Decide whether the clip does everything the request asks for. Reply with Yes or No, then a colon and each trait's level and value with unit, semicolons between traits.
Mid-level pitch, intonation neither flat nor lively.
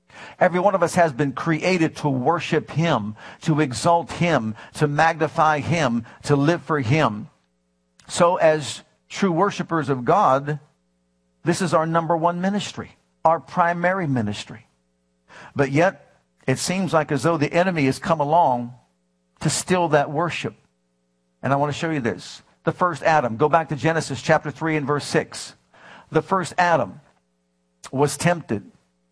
No: medium, 150 Hz; wide, 6.9 semitones